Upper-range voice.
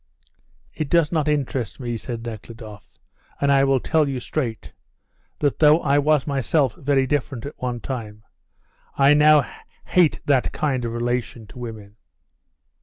No: low, 135 Hz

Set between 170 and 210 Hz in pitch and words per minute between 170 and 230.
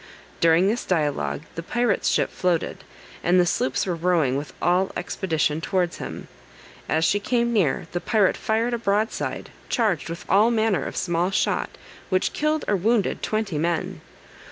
No: medium, 185 Hz; average, 160 wpm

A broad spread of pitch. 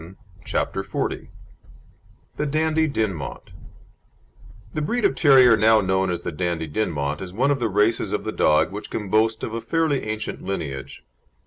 Yes: wide, 6.9 semitones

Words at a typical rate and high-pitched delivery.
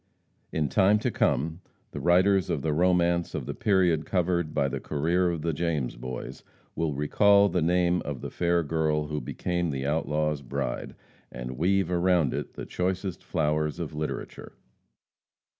No: average, 160 wpm; very low, 85 Hz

